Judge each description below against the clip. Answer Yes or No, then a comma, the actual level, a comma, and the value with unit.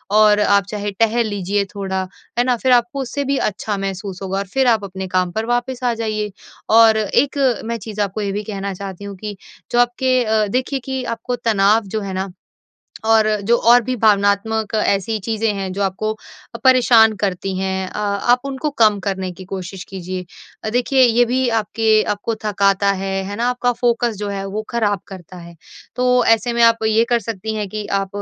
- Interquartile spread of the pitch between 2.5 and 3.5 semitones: Yes, average, 3.2 semitones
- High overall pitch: Yes, high, 215 Hz